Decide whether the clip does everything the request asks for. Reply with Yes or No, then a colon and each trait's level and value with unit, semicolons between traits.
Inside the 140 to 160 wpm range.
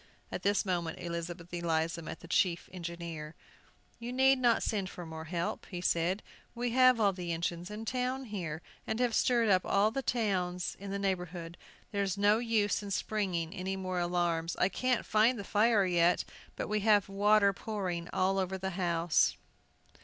No: average, 175 wpm